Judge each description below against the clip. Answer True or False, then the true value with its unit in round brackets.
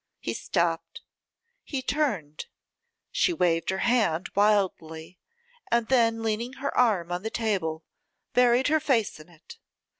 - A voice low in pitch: False (220 Hz)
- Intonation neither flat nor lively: False (6.2 semitones)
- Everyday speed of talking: False (130 wpm)